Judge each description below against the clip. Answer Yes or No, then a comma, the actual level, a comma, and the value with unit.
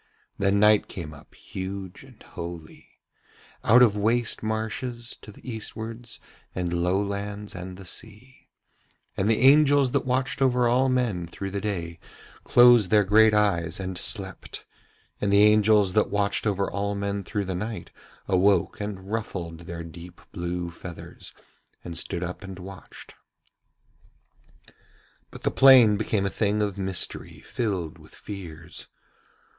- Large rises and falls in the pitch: No, average, 3.3 semitones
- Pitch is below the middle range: Yes, low, 100 Hz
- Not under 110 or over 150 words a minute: Yes, average, 145 wpm